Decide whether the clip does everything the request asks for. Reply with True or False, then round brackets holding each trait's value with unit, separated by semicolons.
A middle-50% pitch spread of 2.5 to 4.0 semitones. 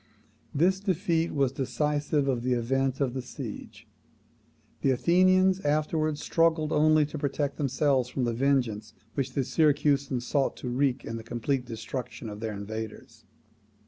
True (3.7 semitones)